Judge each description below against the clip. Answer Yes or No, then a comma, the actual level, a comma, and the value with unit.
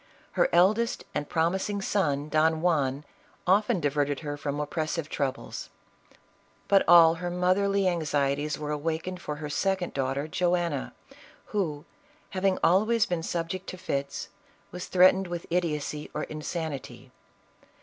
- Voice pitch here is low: No, medium, 165 Hz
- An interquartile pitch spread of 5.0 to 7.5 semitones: No, average, 3.7 semitones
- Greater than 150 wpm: No, average, 140 wpm